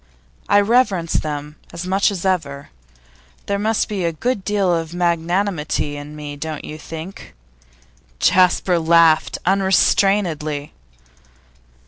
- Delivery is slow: Yes, slow, 115 wpm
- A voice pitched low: No, medium, 170 Hz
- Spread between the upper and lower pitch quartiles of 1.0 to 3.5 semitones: No, average, 4.0 semitones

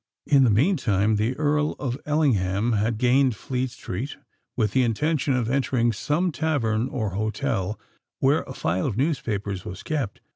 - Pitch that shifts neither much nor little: Yes, average, 4.8 semitones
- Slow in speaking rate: No, average, 155 wpm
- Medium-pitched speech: No, low, 125 Hz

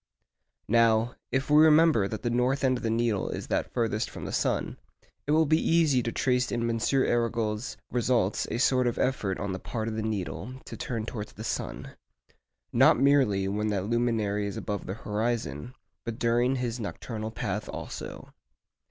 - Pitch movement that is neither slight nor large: Yes, average, 3.0 semitones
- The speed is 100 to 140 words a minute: No, average, 180 wpm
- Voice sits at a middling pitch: No, low, 115 Hz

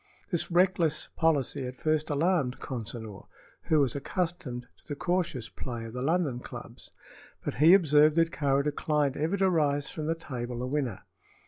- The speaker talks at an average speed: Yes, average, 165 wpm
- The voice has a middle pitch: Yes, medium, 145 Hz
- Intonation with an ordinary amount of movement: Yes, average, 4.5 semitones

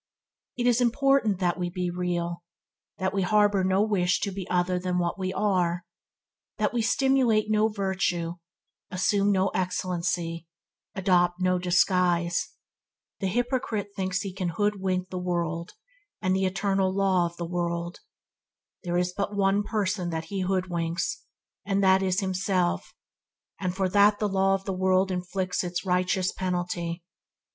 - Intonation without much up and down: Yes, narrow, 1.9 semitones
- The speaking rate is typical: Yes, average, 155 wpm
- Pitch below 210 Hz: Yes, medium, 185 Hz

